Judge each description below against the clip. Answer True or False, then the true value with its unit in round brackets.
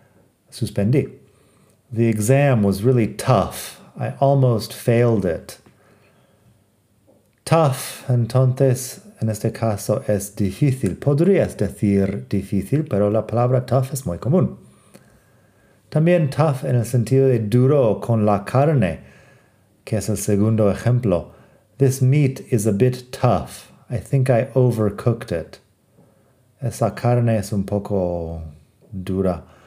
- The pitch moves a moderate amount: True (4.1 semitones)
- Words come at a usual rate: False (120 wpm)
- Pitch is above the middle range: False (115 Hz)